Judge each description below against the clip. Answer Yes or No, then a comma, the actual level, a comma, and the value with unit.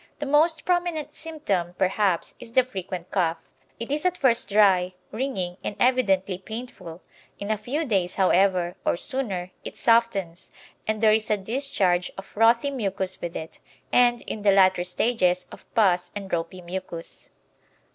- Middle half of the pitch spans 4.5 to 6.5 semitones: Yes, average, 5.1 semitones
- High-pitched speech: Yes, high, 200 Hz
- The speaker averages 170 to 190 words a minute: No, average, 155 wpm